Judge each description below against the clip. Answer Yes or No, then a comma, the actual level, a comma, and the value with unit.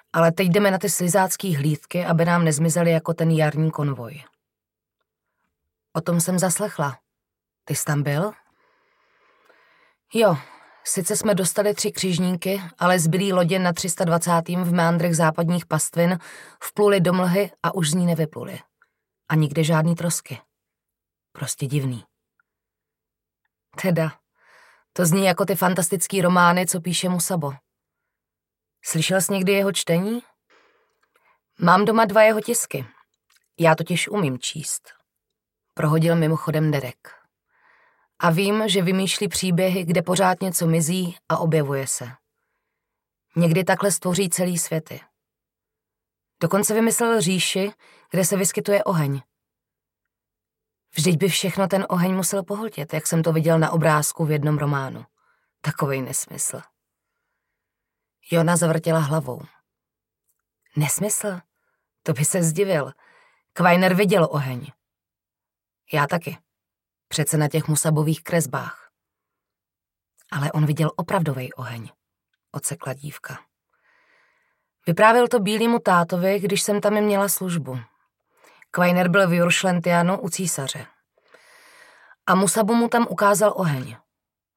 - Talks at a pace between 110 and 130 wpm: Yes, average, 120 wpm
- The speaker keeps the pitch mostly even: No, average, 4.3 semitones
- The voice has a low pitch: No, medium, 175 Hz